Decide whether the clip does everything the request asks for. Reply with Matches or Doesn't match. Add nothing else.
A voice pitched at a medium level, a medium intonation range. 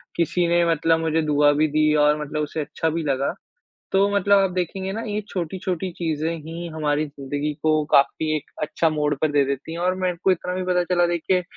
Matches